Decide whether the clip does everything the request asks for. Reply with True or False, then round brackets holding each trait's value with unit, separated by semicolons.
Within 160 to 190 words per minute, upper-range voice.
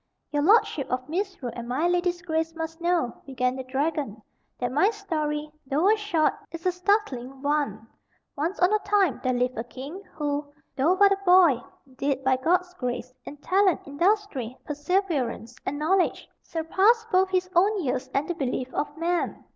True (170 wpm; 310 Hz)